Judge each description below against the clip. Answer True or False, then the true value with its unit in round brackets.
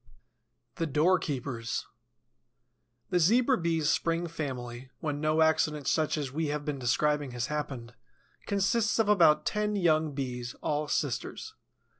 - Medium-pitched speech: True (150 Hz)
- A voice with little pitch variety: False (3.5 semitones)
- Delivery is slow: True (130 wpm)